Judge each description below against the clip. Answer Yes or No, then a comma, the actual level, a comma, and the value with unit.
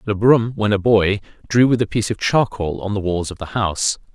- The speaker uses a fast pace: Yes, fast, 245 wpm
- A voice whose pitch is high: No, low, 105 Hz